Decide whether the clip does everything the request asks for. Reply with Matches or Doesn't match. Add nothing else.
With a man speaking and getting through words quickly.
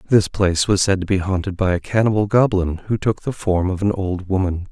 Matches